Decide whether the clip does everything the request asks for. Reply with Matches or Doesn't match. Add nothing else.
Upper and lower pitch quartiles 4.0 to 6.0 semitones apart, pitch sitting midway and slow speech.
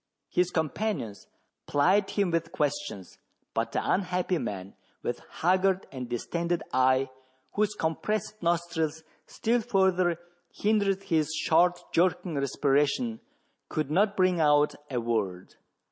Matches